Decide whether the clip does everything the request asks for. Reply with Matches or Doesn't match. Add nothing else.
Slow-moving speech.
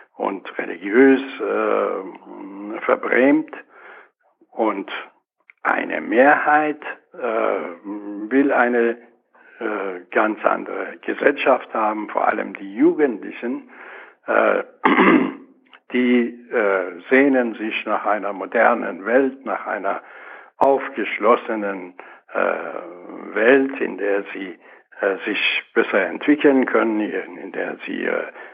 Matches